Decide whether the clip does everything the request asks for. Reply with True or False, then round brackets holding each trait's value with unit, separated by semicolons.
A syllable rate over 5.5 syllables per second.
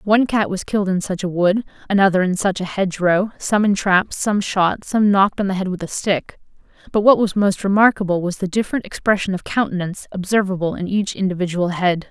True (5.8 syllables/s)